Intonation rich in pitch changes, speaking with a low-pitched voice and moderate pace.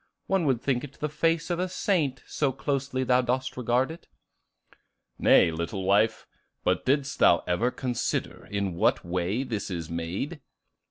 Yes: wide, 6.4 semitones; low, 125 Hz; average, 160 wpm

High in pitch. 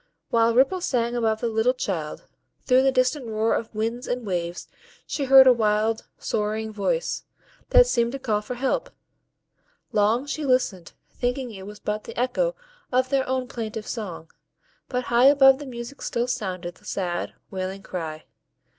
Yes: high, 235 Hz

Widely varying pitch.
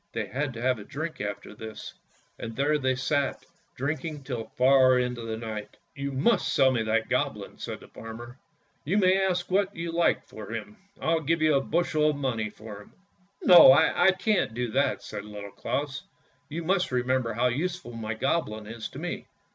Yes: wide, 5.9 semitones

